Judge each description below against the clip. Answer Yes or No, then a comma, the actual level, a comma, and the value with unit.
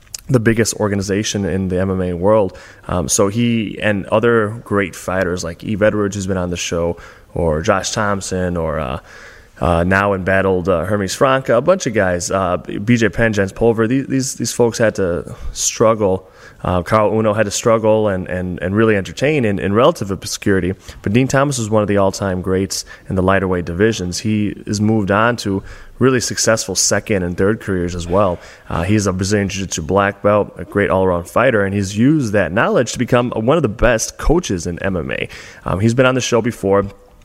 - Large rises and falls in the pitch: No, average, 3.0 semitones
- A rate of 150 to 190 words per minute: No, average, 200 wpm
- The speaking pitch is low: Yes, low, 100 Hz